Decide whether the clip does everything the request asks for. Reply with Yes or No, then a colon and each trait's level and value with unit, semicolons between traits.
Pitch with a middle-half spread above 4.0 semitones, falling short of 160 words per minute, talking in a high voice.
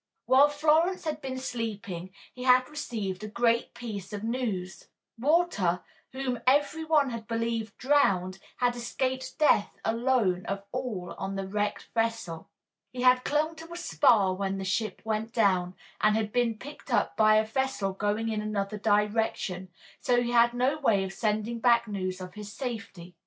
No: average, 4.4 semitones; average, 170 wpm; high, 225 Hz